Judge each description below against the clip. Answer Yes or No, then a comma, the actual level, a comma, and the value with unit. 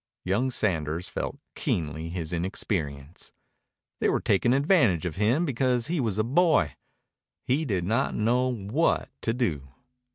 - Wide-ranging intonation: Yes, wide, 6.9 semitones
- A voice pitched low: Yes, low, 110 Hz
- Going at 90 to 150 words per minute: Yes, average, 140 wpm